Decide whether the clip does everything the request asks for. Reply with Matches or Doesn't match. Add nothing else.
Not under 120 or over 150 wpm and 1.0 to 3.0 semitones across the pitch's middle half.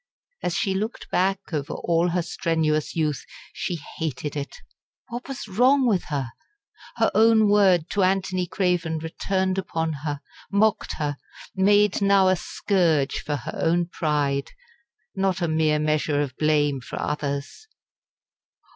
Doesn't match